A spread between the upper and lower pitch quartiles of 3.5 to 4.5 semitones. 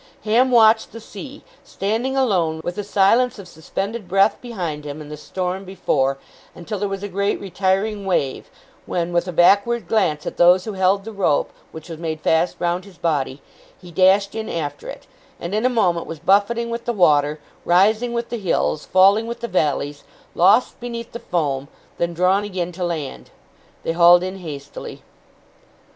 Yes: average, 4.2 semitones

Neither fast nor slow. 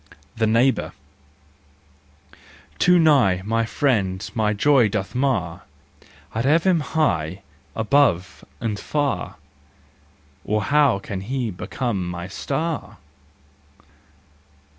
No: slow, 95 wpm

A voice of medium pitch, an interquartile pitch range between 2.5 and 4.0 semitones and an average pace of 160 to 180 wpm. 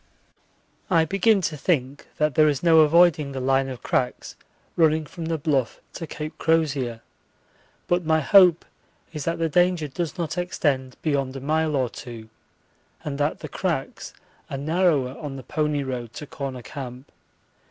Yes: medium, 150 Hz; average, 3.5 semitones; average, 165 wpm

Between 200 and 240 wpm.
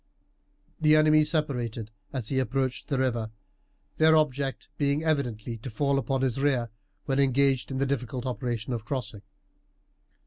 No: average, 145 wpm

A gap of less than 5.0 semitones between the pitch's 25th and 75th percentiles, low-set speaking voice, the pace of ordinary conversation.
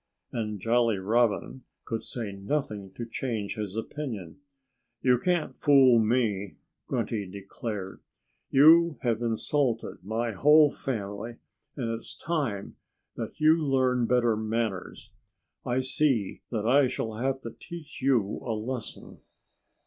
No: average, 3.8 semitones; low, 115 Hz; slow, 125 wpm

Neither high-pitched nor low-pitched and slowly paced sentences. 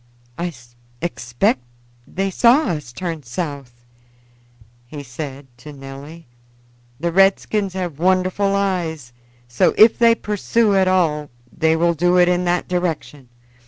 Yes: medium, 170 Hz; slow, 125 wpm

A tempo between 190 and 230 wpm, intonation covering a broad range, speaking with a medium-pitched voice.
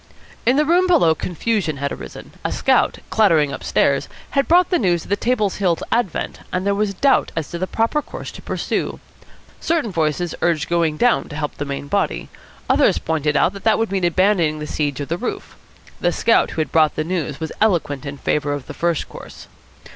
Yes: fast, 205 wpm; wide, 6.0 semitones; medium, 170 Hz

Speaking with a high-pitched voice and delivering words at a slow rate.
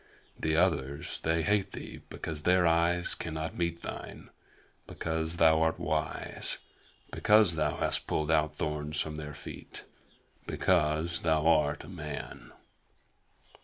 No: very low, 80 Hz; slow, 130 wpm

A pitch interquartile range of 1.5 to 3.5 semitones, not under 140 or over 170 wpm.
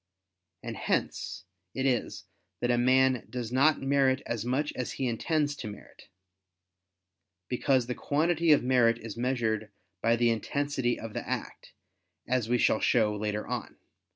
Yes: average, 2.9 semitones; average, 155 wpm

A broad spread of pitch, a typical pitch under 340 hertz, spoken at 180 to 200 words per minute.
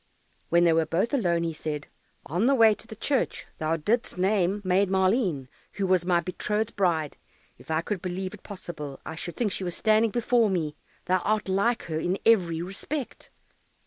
No: average, 4.3 semitones; medium, 185 Hz; average, 185 wpm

